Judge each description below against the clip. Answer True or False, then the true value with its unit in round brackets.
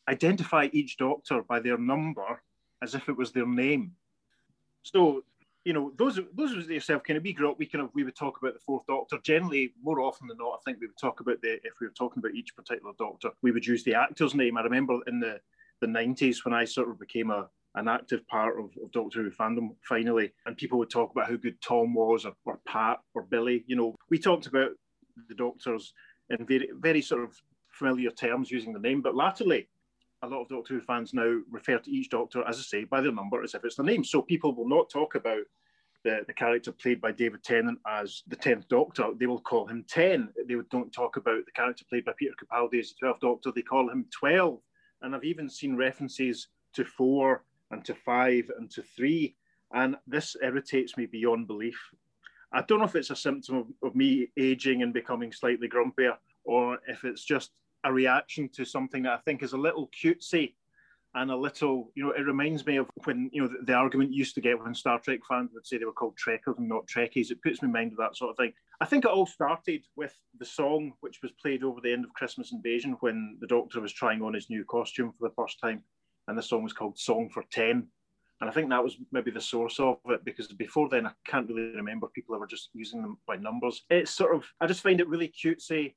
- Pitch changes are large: False (4.7 semitones)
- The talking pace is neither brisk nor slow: False (235 wpm)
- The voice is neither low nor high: False (130 Hz)